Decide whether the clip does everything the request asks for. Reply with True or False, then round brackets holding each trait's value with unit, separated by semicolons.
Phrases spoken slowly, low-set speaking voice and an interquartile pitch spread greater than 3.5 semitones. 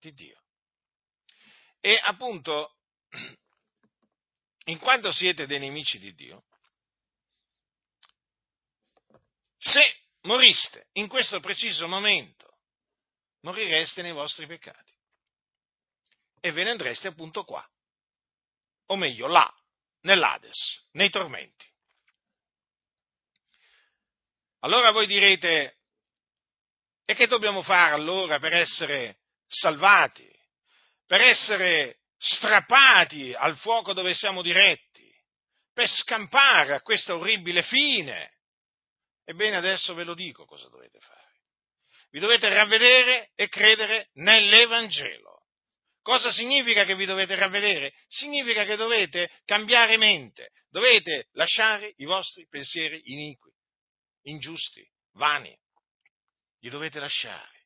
False (95 wpm; 205 Hz; 5.1 semitones)